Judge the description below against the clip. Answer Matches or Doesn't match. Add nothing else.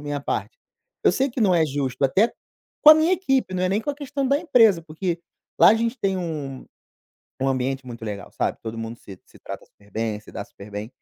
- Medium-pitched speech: Matches